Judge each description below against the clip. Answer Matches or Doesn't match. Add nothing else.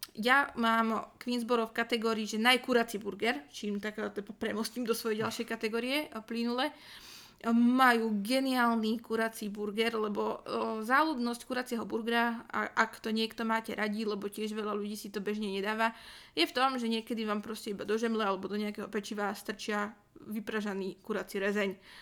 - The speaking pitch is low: Doesn't match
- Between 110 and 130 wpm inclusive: Doesn't match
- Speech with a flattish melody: Matches